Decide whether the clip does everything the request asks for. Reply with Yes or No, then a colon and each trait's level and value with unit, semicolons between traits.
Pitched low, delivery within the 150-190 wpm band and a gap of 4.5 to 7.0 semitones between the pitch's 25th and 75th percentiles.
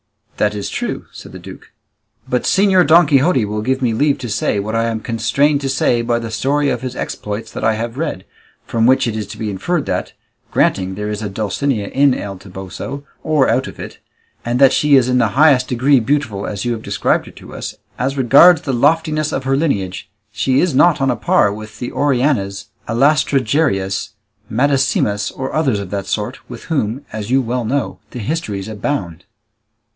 No: low, 125 Hz; average, 200 wpm; average, 4.9 semitones